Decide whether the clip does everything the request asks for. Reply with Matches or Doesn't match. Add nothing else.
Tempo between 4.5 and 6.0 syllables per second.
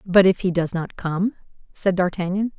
Matches